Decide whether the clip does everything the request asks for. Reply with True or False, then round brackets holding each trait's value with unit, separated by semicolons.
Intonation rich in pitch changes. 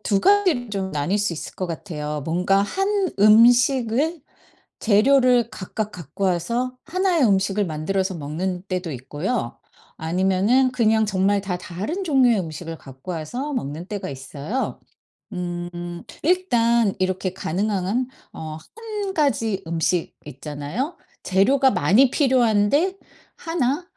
True (6.5 semitones)